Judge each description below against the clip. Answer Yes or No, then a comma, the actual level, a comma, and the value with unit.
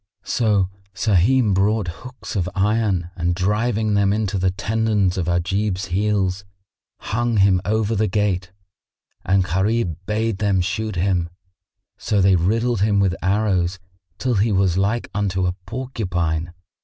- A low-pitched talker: Yes, low, 100 Hz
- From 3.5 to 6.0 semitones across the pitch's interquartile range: No, average, 2.9 semitones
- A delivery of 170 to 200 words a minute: No, average, 140 wpm